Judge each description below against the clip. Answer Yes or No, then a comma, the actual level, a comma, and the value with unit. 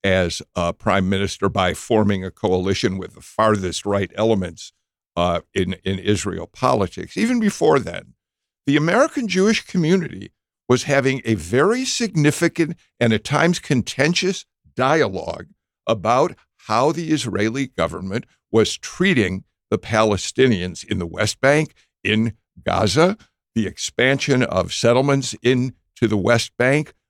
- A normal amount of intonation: No, wide, 6.3 semitones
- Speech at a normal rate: No, slow, 130 wpm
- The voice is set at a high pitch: No, low, 115 Hz